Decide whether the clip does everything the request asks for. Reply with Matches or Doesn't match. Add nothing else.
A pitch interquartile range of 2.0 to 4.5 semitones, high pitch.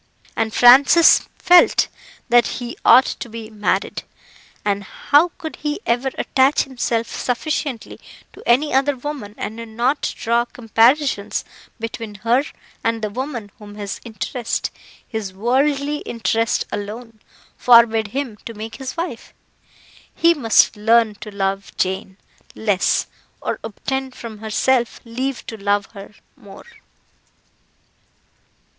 Matches